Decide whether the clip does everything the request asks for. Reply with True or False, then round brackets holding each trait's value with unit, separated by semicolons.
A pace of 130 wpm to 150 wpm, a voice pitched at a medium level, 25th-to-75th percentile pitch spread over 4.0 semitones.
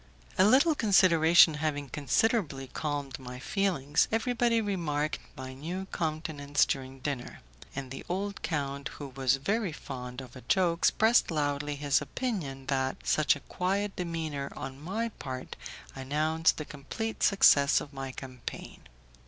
True (135 wpm; 150 Hz; 5.5 semitones)